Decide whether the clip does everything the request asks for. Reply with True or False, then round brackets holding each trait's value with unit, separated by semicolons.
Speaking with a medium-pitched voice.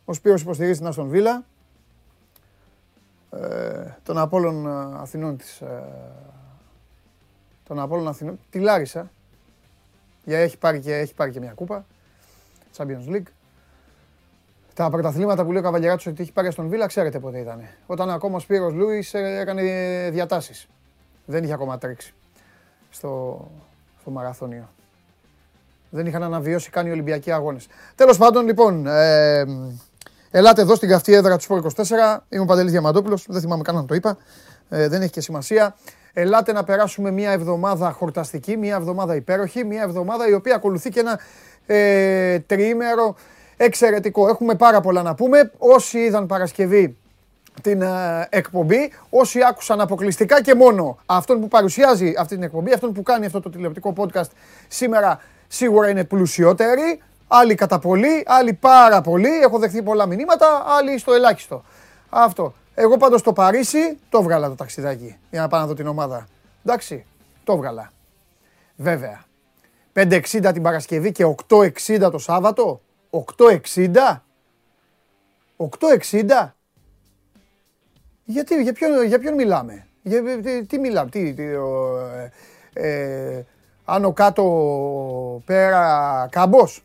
True (180 Hz)